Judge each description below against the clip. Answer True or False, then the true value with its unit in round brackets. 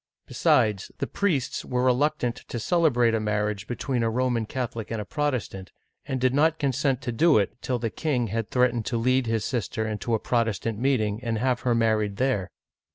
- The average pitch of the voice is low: True (120 Hz)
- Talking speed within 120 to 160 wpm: False (190 wpm)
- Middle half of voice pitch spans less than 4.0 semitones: True (2.9 semitones)